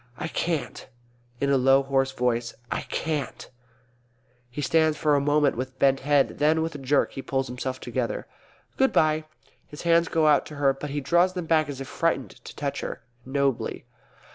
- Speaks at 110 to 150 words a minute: No, average, 190 wpm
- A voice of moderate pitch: Yes, medium, 145 Hz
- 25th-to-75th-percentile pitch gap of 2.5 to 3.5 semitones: Yes, average, 2.8 semitones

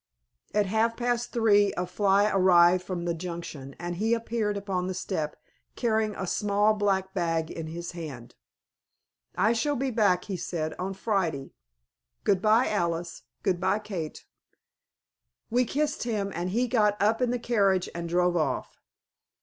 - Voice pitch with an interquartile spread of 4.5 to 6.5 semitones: No, average, 4.1 semitones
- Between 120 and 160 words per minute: Yes, average, 150 wpm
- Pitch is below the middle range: No, high, 195 Hz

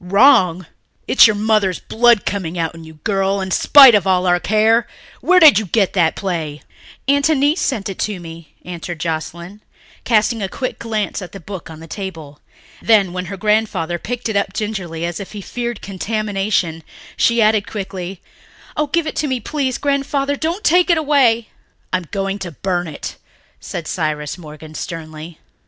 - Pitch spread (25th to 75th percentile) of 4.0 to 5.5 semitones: Yes, average, 4.9 semitones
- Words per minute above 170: Yes, average, 180 wpm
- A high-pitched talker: Yes, high, 195 Hz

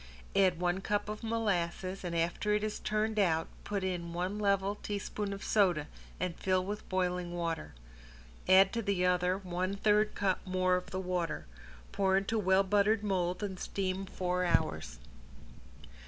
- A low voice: No, high, 190 Hz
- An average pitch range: No, narrow, 2.2 semitones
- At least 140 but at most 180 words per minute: Yes, average, 160 wpm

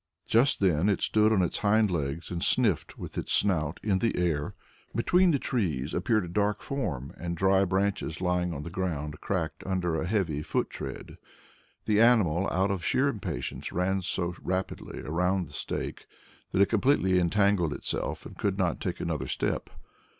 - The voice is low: Yes, very low, 95 Hz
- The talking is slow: No, average, 170 wpm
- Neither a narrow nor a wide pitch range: Yes, average, 3.4 semitones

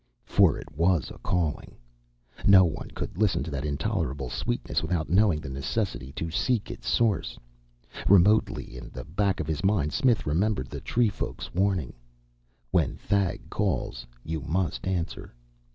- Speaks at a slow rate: No, average, 150 wpm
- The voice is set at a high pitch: No, very low, 85 Hz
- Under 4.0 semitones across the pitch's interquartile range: No, average, 5.3 semitones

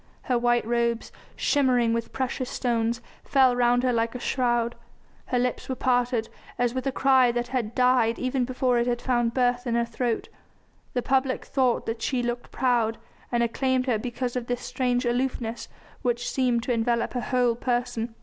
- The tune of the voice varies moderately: No, narrow, 1.3 semitones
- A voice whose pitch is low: No, high, 245 Hz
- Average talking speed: Yes, average, 180 wpm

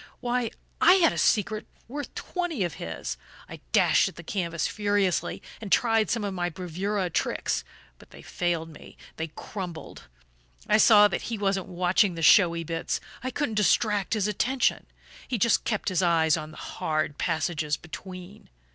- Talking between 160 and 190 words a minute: Yes, average, 165 wpm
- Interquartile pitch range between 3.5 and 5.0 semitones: Yes, average, 4.3 semitones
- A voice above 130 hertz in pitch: Yes, high, 190 Hz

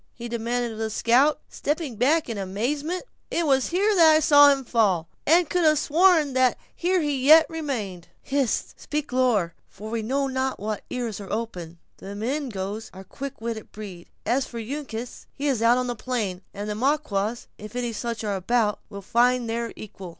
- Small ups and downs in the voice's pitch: No, average, 5.0 semitones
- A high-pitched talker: Yes, high, 240 Hz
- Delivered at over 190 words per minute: Yes, average, 200 wpm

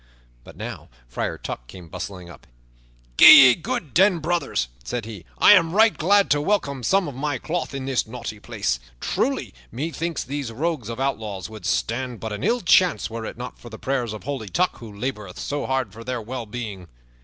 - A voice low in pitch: Yes, low, 125 Hz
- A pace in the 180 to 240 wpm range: Yes, average, 200 wpm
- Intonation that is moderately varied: No, wide, 5.9 semitones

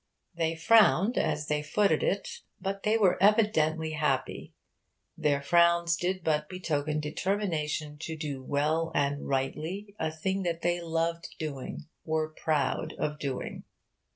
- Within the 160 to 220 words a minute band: No, slow, 135 wpm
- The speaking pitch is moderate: Yes, medium, 160 Hz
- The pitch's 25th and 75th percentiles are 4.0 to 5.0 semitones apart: No, average, 2.9 semitones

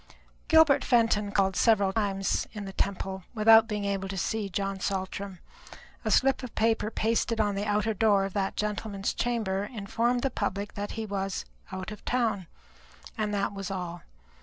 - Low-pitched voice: No, high, 205 Hz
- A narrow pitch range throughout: Yes, narrow, 2.3 semitones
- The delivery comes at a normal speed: Yes, average, 170 wpm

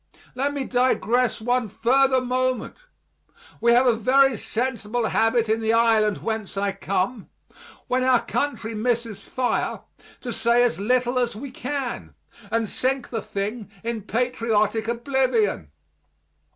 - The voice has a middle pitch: No, high, 235 Hz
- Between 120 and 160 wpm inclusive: Yes, slow, 135 wpm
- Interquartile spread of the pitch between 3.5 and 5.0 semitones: No, narrow, 2.6 semitones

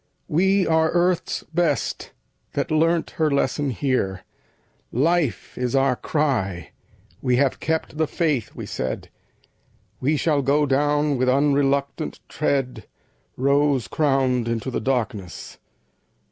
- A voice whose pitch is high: No, medium, 140 Hz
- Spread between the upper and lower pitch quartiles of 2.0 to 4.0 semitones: Yes, average, 3.3 semitones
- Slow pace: Yes, slow, 120 wpm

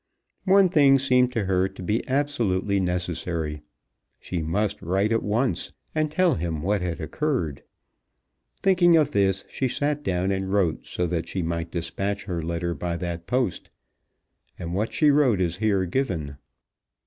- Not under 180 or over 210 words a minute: No, average, 160 wpm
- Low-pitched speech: Yes, very low, 95 Hz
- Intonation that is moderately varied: No, wide, 7.0 semitones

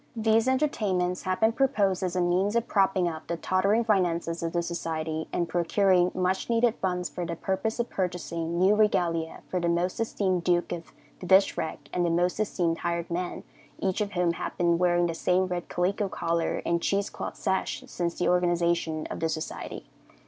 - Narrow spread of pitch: Yes, narrow, 2.3 semitones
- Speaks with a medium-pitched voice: Yes, medium, 180 Hz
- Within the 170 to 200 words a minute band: Yes, average, 190 wpm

